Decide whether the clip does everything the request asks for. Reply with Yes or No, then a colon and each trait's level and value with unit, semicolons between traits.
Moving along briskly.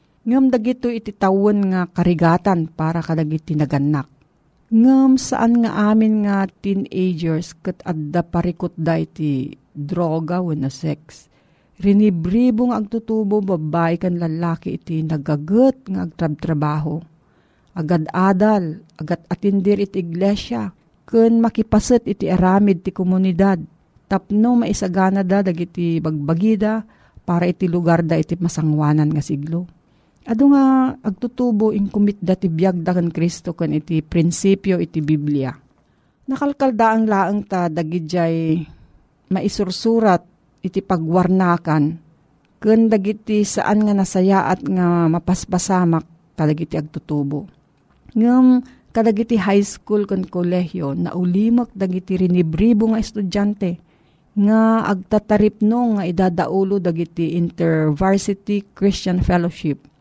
No: slow, 110 wpm